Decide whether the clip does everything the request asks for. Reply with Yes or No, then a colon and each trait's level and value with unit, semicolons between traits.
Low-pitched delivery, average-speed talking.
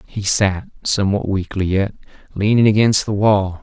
Yes: low, 100 Hz; average, 150 wpm